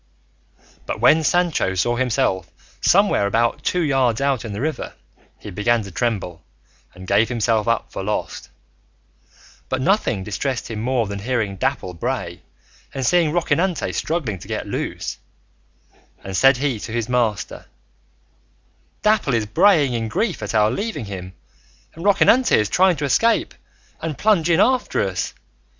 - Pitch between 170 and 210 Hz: No, low, 125 Hz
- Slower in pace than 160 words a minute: Yes, average, 150 wpm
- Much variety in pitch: Yes, wide, 7.3 semitones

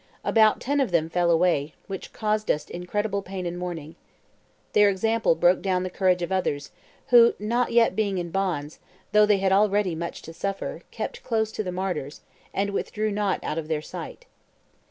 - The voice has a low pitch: No, high, 190 Hz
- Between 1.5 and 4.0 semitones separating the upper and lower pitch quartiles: Yes, average, 3.5 semitones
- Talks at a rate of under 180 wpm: No, average, 190 wpm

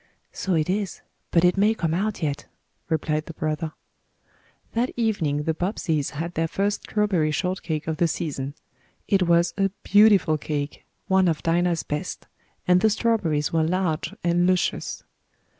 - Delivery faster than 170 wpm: No, average, 155 wpm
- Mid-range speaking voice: Yes, medium, 170 Hz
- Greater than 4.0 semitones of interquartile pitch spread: No, average, 3.6 semitones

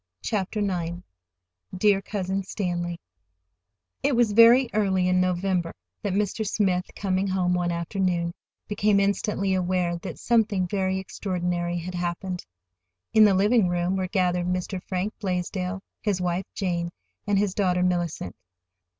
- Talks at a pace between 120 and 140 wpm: Yes, slow, 135 wpm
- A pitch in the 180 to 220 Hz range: Yes, medium, 185 Hz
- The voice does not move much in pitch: Yes, narrow, 2.1 semitones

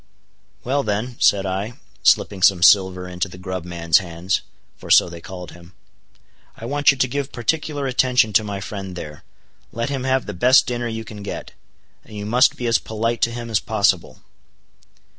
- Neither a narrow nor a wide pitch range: Yes, average, 4.7 semitones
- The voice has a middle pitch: No, low, 105 Hz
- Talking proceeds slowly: No, average, 185 wpm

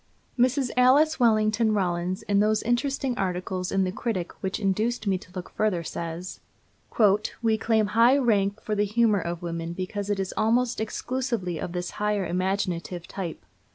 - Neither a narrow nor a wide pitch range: Yes, average, 4.0 semitones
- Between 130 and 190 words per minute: Yes, average, 160 wpm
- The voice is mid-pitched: No, high, 205 Hz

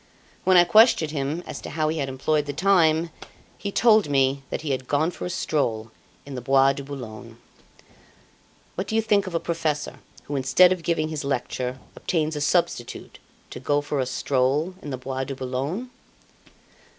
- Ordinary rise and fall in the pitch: Yes, average, 4.0 semitones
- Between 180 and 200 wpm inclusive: Yes, average, 185 wpm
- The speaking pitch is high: No, medium, 145 Hz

